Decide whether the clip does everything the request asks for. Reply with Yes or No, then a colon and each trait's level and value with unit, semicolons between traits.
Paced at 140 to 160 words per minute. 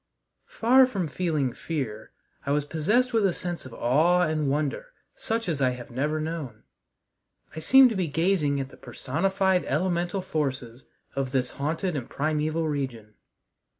Yes: average, 155 wpm